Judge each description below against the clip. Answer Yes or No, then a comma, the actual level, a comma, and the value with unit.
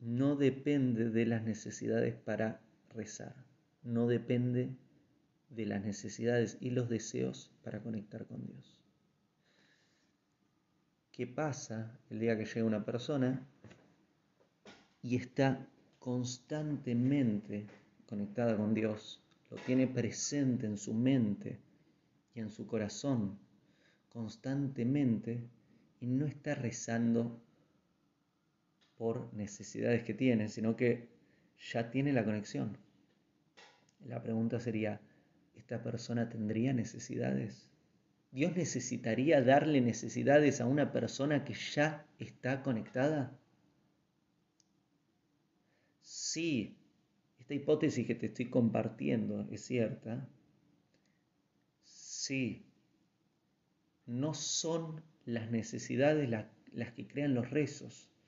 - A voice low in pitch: Yes, low, 120 Hz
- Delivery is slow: Yes, slow, 100 wpm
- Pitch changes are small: No, average, 3.8 semitones